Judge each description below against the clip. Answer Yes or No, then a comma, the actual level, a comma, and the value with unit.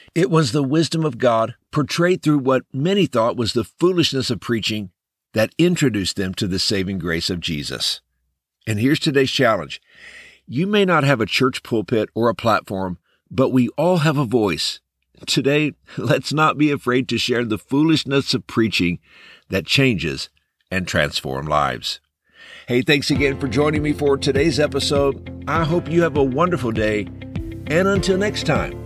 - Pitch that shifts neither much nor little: No, wide, 5.8 semitones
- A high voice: No, low, 135 Hz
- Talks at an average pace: Yes, average, 170 wpm